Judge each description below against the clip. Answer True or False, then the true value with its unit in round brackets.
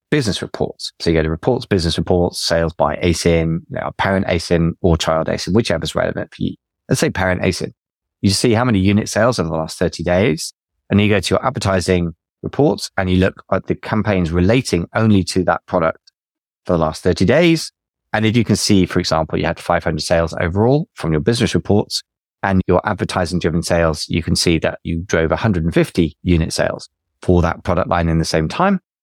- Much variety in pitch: False (3.8 semitones)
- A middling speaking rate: False (215 wpm)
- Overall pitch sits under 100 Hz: True (90 Hz)